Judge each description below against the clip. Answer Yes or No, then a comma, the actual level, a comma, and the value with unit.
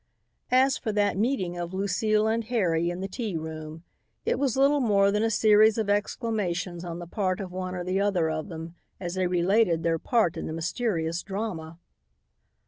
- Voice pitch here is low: No, high, 190 Hz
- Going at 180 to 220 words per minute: Yes, average, 190 wpm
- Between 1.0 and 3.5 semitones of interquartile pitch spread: No, average, 4.2 semitones